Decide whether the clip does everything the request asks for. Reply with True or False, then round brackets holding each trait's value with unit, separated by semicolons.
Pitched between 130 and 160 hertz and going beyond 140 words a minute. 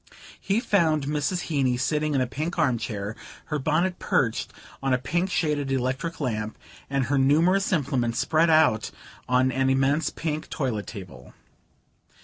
True (140 Hz; 150 wpm)